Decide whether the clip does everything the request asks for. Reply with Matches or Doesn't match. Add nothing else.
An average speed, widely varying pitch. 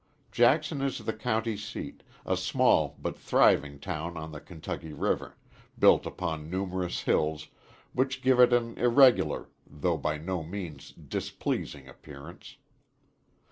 Doesn't match